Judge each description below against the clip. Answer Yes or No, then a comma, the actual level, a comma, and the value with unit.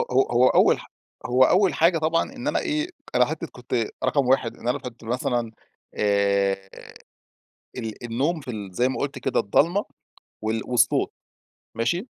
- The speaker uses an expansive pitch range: Yes, wide, 5.8 semitones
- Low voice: Yes, low, 125 Hz